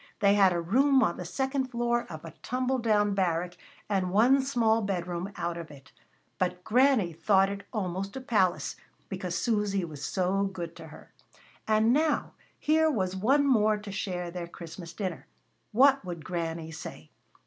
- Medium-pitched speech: No, high, 195 Hz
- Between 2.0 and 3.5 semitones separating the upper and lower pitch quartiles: No, average, 5.3 semitones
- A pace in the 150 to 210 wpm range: Yes, average, 170 wpm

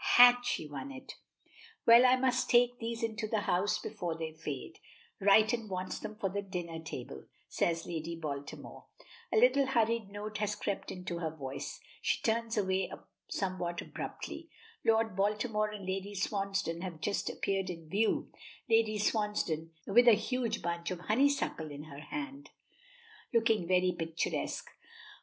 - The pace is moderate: Yes, average, 150 wpm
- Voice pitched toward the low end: No, high, 200 Hz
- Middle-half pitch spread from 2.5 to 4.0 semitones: No, average, 4.8 semitones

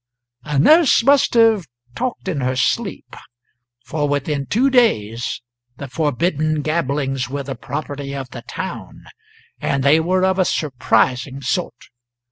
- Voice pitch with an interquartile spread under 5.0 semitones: No, wide, 5.5 semitones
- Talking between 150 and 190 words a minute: No, slow, 135 wpm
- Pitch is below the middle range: No, medium, 145 Hz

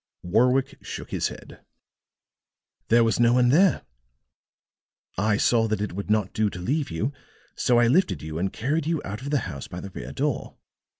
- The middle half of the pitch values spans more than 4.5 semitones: Yes, average, 5.1 semitones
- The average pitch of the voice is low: Yes, low, 115 Hz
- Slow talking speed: No, average, 185 wpm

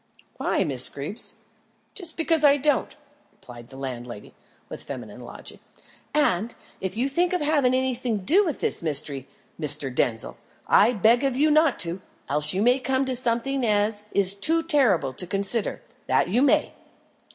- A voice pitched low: No, high, 230 Hz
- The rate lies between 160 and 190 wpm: Yes, average, 165 wpm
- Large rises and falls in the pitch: Yes, wide, 8.7 semitones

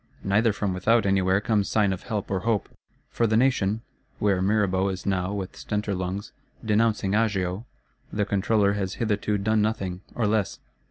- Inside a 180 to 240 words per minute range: No, average, 165 wpm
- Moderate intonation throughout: No, narrow, 2.2 semitones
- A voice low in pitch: Yes, low, 100 Hz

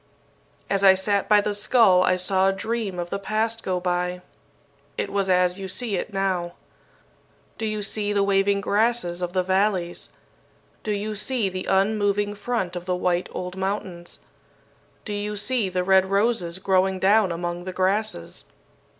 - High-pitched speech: Yes, high, 195 Hz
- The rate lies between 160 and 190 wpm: Yes, average, 165 wpm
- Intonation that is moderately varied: No, narrow, 2.3 semitones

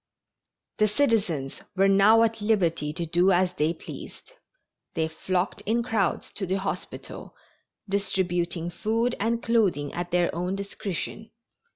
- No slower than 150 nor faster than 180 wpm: No, slow, 135 wpm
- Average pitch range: Yes, average, 3.7 semitones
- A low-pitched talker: No, high, 190 Hz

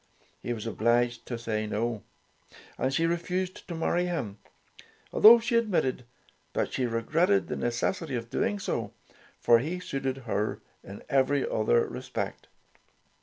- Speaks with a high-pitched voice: No, low, 130 Hz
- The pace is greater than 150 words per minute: No, average, 140 wpm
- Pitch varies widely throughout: Yes, wide, 7.0 semitones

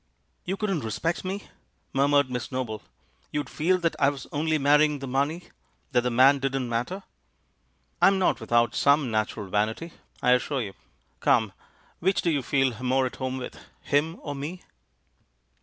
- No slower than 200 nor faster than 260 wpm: No, average, 175 wpm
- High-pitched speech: No, medium, 140 Hz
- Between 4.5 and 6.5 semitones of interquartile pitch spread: No, average, 4.0 semitones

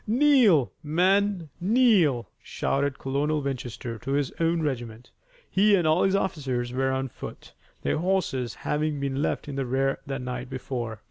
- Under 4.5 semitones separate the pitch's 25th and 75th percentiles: No, average, 5.3 semitones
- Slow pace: No, average, 155 wpm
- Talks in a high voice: No, medium, 140 Hz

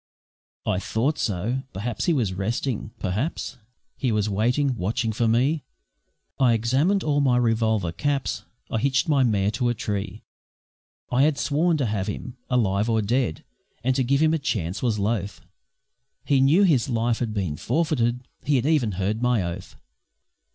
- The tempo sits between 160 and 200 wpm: Yes, average, 170 wpm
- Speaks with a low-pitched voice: Yes, low, 120 Hz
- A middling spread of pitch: Yes, average, 4.6 semitones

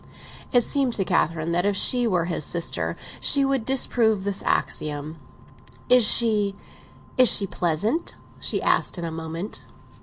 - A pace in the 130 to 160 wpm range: Yes, average, 145 wpm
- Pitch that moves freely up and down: Yes, wide, 6.3 semitones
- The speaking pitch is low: No, high, 200 Hz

